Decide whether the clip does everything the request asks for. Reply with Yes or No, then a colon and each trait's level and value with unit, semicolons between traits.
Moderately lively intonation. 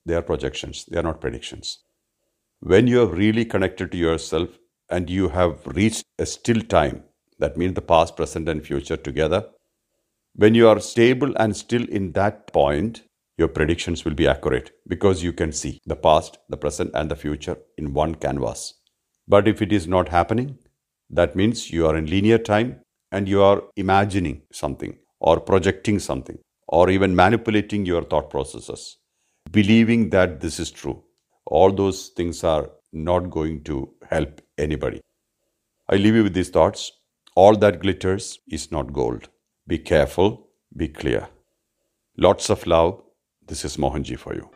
Yes: average, 4.1 semitones